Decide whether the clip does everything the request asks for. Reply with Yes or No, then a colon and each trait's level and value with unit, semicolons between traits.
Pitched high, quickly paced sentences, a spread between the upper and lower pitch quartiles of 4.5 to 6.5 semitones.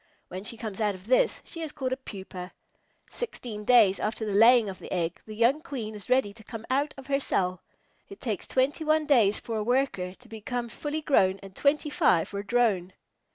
Yes: high, 230 Hz; fast, 215 wpm; average, 5.1 semitones